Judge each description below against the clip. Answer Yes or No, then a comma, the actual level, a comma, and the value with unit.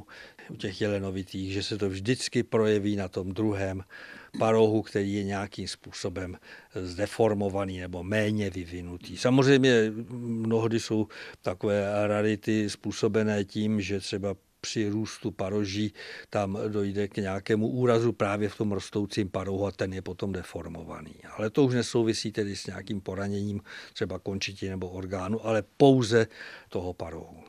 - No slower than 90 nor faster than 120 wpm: No, average, 140 wpm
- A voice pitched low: Yes, low, 105 Hz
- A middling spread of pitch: No, narrow, 2.3 semitones